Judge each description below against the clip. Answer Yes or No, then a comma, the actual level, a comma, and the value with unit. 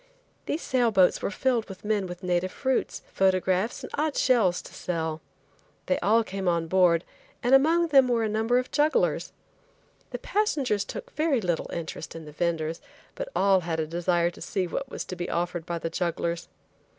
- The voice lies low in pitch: No, high, 190 Hz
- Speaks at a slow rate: No, average, 185 wpm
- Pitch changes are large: Yes, wide, 6.6 semitones